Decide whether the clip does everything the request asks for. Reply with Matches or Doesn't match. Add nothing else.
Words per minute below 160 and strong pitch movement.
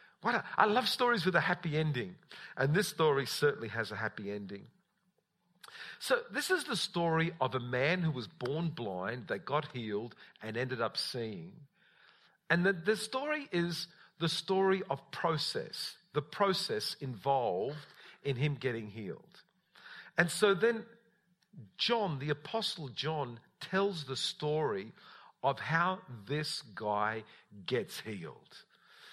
Matches